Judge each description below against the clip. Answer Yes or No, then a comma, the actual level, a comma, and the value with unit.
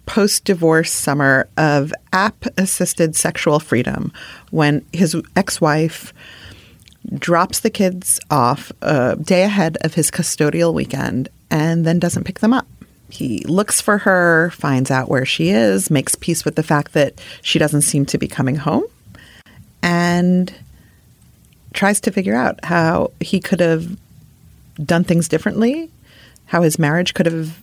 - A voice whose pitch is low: No, medium, 170 Hz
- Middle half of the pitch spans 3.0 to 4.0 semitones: Yes, average, 3.4 semitones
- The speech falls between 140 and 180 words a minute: Yes, average, 150 wpm